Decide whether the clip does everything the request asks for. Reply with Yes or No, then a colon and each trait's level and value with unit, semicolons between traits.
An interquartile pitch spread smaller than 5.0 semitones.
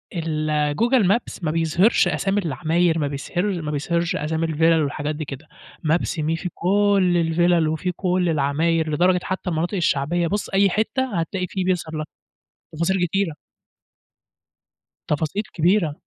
Yes: average, 3.0 semitones